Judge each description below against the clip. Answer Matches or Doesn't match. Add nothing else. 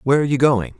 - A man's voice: Matches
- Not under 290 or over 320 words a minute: Matches